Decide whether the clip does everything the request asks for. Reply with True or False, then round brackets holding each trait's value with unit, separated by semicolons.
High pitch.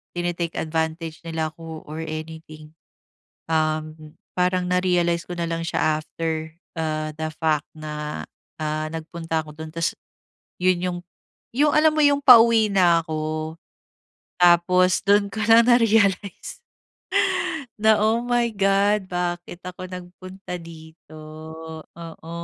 False (170 Hz)